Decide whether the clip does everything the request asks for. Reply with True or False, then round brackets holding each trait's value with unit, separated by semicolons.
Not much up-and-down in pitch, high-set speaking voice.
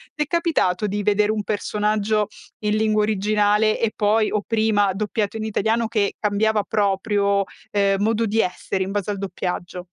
True (1.3 semitones; 210 Hz)